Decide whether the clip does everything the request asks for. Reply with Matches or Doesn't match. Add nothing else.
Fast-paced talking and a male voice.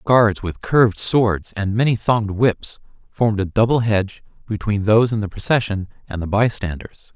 Doesn't match